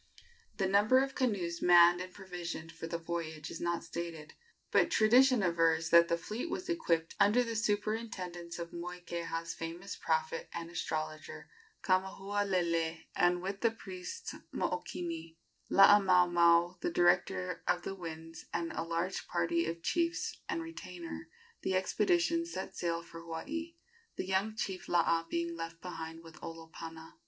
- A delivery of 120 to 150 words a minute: Yes, average, 145 wpm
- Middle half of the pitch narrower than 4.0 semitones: Yes, average, 3.0 semitones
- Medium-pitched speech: Yes, medium, 175 Hz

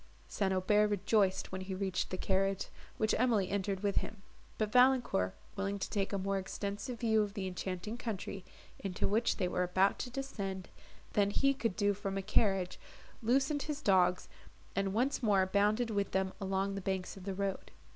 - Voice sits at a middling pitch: No, high, 200 Hz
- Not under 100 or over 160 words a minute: No, average, 185 wpm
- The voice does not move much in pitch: Yes, narrow, 2.2 semitones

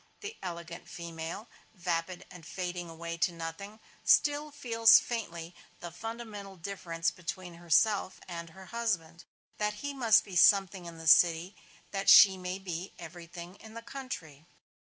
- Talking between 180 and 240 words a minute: No, average, 145 wpm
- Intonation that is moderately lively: Yes, average, 3.9 semitones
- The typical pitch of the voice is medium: Yes, medium, 180 Hz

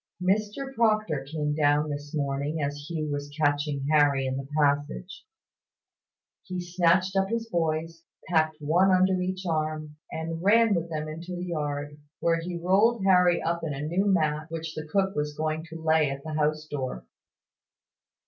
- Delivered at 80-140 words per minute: No, average, 165 wpm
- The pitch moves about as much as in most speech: Yes, average, 3.4 semitones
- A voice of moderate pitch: Yes, medium, 160 Hz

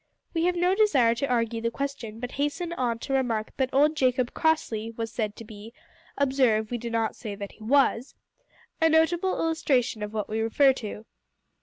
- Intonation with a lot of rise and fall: No, average, 4.3 semitones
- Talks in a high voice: Yes, high, 245 Hz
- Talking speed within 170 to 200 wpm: Yes, average, 190 wpm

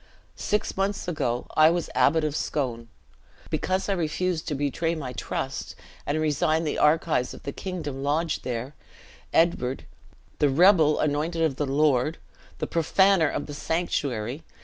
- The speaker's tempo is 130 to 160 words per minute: Yes, average, 150 wpm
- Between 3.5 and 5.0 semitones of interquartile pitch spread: No, average, 3.1 semitones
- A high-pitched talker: No, medium, 155 Hz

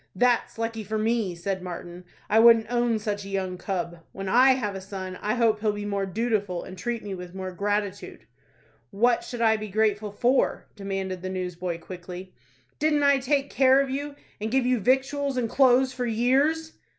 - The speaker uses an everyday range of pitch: Yes, average, 4.5 semitones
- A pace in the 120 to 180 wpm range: No, average, 190 wpm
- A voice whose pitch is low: No, high, 215 Hz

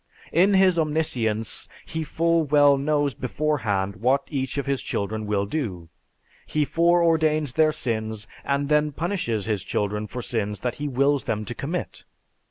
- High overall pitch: No, medium, 140 Hz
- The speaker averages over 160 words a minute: No, average, 155 wpm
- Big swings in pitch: Yes, wide, 5.9 semitones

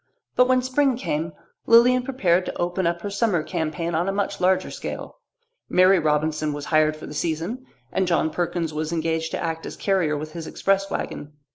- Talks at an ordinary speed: Yes, average, 190 wpm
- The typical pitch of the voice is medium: Yes, medium, 170 Hz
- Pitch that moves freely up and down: No, average, 3.9 semitones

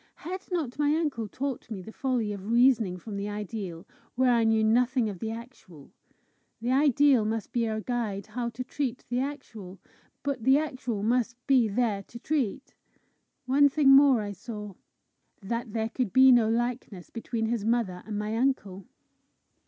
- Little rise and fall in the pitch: No, average, 3.6 semitones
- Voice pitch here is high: Yes, high, 235 Hz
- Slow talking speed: No, average, 170 wpm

